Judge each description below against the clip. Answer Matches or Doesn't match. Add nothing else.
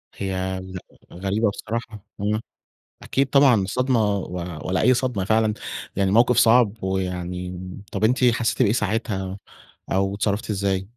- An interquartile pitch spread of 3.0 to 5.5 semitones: Matches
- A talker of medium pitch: Doesn't match